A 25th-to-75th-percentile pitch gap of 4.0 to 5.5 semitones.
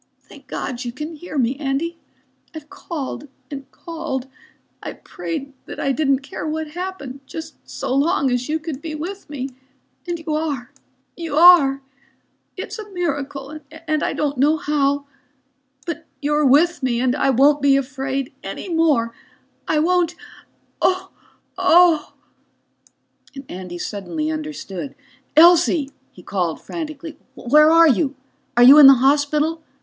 No: average, 3.1 semitones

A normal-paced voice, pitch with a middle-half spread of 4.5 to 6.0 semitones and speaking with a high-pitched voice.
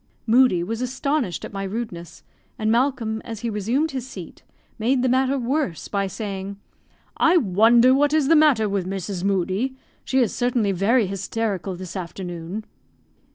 Yes: average, 155 wpm; average, 4.9 semitones; high, 220 Hz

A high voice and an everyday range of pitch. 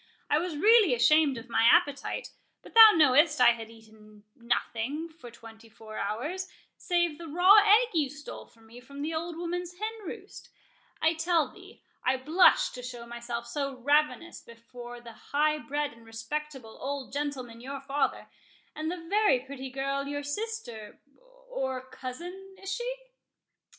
No: very high, 285 Hz; wide, 5.8 semitones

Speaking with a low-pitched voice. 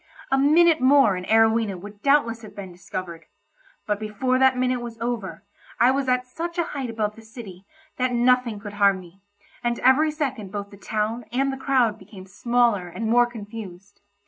No: high, 230 Hz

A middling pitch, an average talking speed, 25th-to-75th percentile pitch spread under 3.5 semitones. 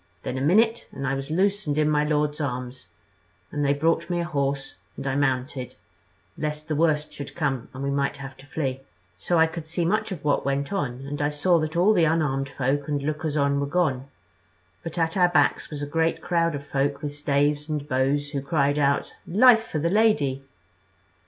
No: medium, 145 Hz; fast, 210 wpm; average, 2.9 semitones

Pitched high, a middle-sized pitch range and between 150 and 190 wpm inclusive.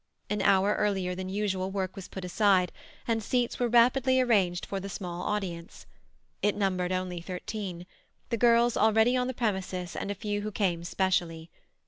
Yes: high, 195 Hz; average, 3.3 semitones; average, 165 wpm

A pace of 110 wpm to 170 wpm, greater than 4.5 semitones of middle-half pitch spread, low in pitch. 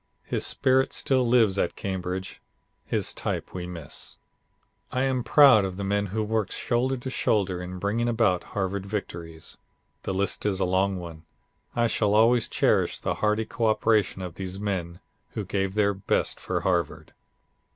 No: average, 165 wpm; average, 3.4 semitones; low, 100 Hz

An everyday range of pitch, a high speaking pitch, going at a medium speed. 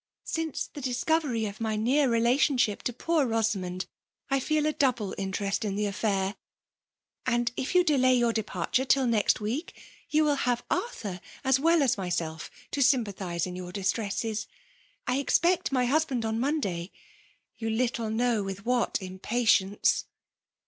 Yes: average, 4.9 semitones; high, 235 Hz; average, 160 wpm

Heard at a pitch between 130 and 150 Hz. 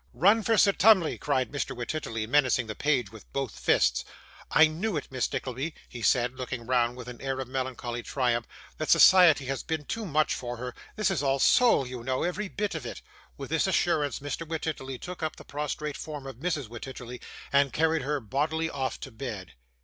Yes: low, 135 Hz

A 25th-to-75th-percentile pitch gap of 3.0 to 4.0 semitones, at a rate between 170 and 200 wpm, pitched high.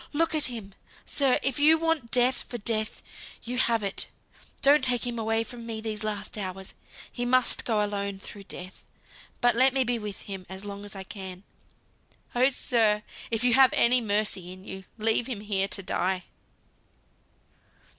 Yes: average, 3.7 semitones; average, 175 wpm; high, 220 Hz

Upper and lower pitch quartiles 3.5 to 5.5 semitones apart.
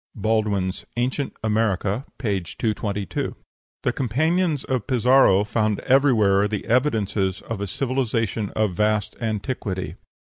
Yes: average, 4.0 semitones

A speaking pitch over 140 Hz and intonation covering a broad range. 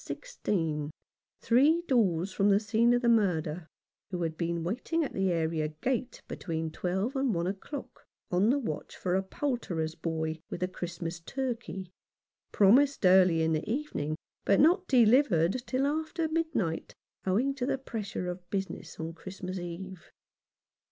Yes: high, 190 Hz; wide, 7.1 semitones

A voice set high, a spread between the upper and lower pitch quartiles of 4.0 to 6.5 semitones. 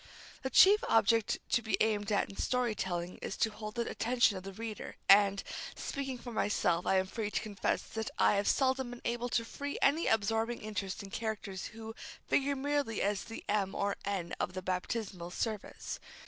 No: high, 220 Hz; average, 3.3 semitones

